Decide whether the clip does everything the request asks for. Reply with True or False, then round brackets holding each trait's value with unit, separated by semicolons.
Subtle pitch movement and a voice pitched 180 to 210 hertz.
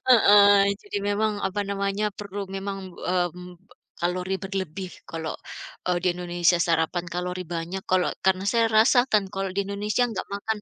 True (2.3 semitones; 190 Hz)